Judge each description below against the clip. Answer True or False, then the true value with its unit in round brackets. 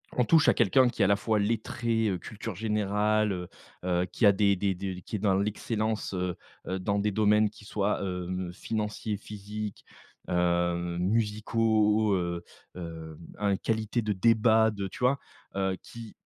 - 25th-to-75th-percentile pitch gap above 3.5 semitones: False (2.8 semitones)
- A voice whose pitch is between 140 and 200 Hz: False (105 Hz)